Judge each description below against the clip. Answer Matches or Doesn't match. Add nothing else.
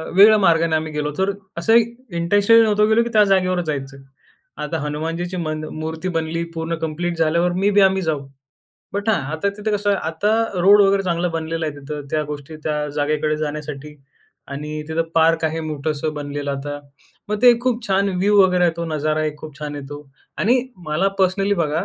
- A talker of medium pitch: Matches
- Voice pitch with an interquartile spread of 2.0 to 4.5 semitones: Matches